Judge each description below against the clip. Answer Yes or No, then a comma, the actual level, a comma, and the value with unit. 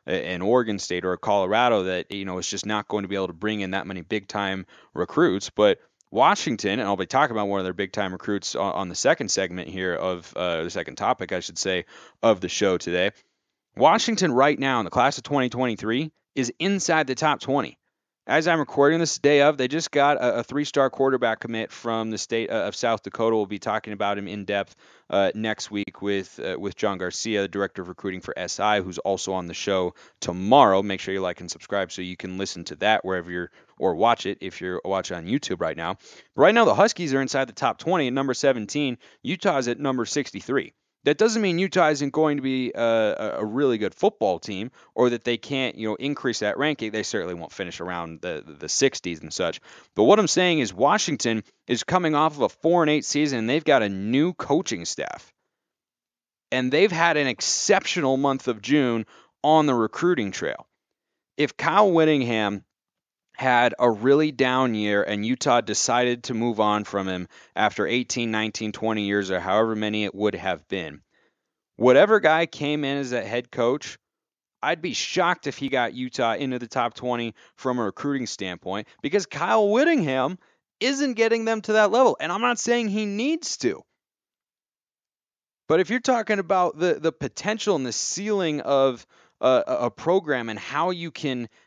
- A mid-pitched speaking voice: No, low, 125 Hz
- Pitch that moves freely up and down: Yes, wide, 6.6 semitones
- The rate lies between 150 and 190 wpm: No, fast, 205 wpm